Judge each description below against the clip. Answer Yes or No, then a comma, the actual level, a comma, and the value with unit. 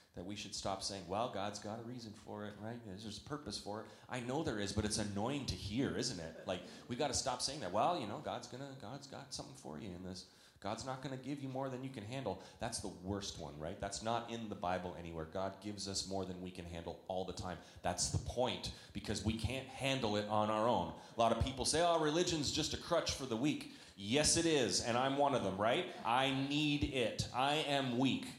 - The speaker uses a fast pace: Yes, fast, 250 wpm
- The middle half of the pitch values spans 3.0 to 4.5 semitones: No, average, 5.1 semitones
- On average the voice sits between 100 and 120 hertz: Yes, low, 105 Hz